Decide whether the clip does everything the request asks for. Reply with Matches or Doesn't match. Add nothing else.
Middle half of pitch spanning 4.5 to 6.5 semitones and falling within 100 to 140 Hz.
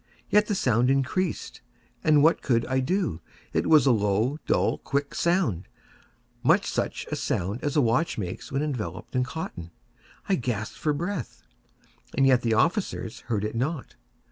Matches